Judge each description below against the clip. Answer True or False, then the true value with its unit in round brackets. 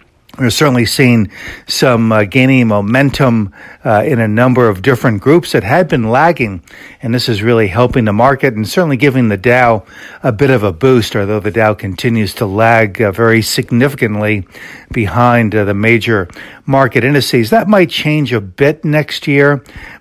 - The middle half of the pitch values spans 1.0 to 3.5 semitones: False (3.9 semitones)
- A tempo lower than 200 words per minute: True (170 wpm)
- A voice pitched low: True (120 Hz)